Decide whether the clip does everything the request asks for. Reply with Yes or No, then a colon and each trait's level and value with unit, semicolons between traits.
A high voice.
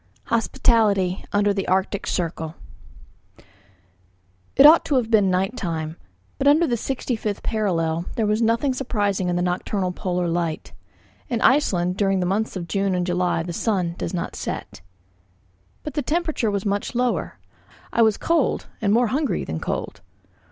Yes: high, 200 Hz